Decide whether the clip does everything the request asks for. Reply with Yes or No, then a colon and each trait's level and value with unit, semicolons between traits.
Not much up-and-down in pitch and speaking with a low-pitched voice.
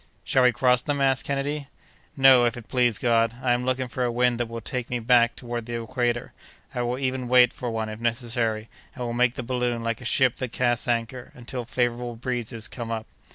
Yes: narrow, 1.4 semitones; low, 120 Hz